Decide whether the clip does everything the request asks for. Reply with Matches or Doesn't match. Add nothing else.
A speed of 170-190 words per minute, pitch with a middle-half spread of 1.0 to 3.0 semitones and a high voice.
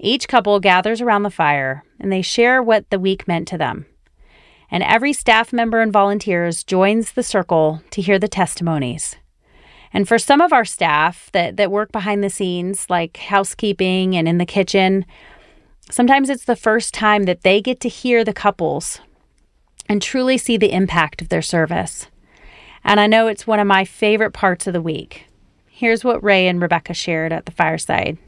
Doesn't match